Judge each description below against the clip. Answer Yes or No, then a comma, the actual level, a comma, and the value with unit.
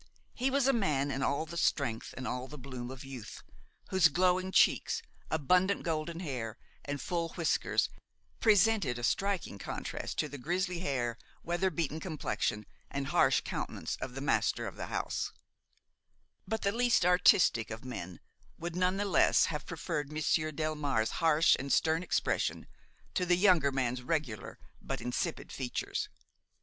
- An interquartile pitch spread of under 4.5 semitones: No, wide, 5.4 semitones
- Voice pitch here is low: No, medium, 155 Hz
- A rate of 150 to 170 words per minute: Yes, average, 155 wpm